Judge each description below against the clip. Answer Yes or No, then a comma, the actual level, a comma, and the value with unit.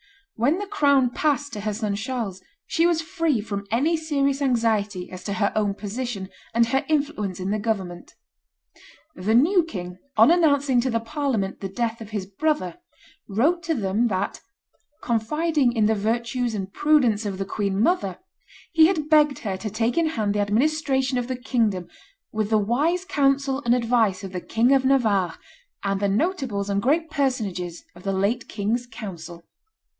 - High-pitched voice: Yes, high, 230 Hz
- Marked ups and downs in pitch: Yes, wide, 5.8 semitones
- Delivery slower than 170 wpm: No, average, 175 wpm